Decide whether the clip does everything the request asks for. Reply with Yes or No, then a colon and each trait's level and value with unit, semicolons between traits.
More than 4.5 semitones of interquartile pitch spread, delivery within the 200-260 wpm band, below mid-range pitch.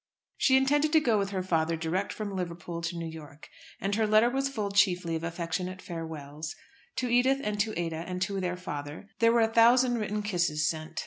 No: average, 5.2 semitones; fast, 205 wpm; medium, 185 Hz